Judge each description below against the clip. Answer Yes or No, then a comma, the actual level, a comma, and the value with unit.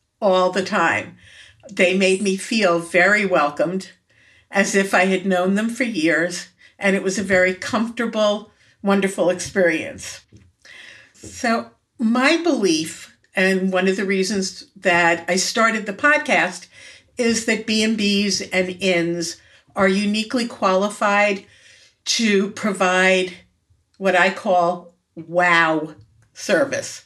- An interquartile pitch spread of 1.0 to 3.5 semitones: Yes, average, 2.8 semitones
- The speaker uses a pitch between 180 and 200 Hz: Yes, high, 190 Hz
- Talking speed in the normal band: No, slow, 120 wpm